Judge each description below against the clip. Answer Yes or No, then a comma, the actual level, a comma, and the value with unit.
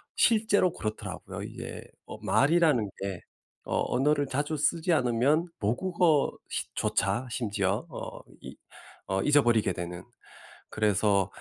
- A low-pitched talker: Yes, low, 125 Hz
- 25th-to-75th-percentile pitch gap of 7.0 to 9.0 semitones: Yes, wide, 7.3 semitones